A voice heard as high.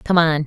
No: medium, 160 Hz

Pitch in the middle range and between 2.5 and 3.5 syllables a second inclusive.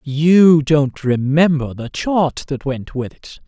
Yes: medium, 145 Hz; 3.4 syllables/s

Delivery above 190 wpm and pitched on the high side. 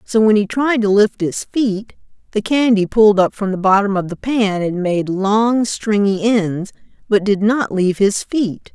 Yes: average, 200 wpm; high, 205 Hz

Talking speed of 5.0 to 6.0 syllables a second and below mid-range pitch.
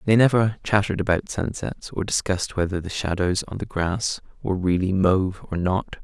Yes: 5.4 syllables/s; very low, 95 Hz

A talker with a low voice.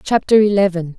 No: high, 195 Hz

